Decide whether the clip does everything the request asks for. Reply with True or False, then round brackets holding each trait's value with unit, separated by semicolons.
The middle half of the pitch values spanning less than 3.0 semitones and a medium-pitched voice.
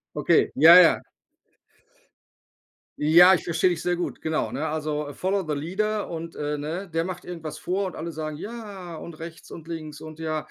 True (2.5 semitones; 165 Hz)